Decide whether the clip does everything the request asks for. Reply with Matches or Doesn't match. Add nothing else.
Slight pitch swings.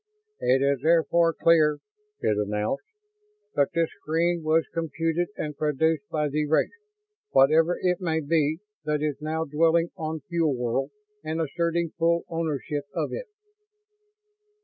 Matches